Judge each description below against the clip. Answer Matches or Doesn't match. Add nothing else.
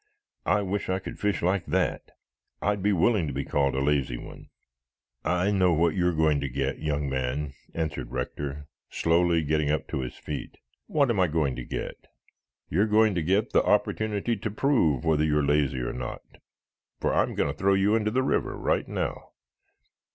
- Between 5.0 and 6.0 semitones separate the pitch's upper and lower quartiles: Matches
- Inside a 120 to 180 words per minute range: Doesn't match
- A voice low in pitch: Matches